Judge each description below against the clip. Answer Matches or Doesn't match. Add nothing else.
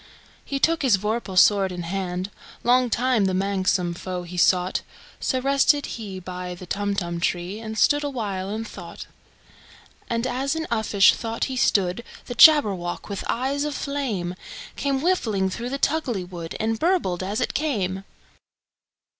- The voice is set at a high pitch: Matches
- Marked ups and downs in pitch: Matches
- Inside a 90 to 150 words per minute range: Matches